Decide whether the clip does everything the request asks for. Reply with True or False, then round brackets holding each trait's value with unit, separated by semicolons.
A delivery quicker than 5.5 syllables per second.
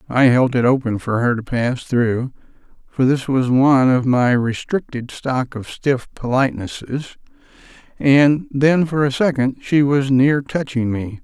False (4.3 syllables/s)